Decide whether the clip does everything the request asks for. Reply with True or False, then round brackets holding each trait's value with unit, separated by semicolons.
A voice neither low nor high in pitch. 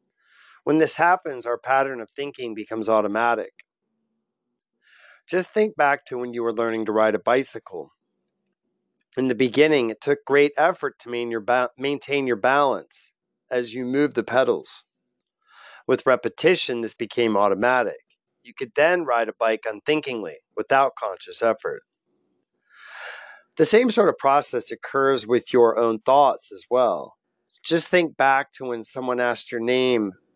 False (130 Hz)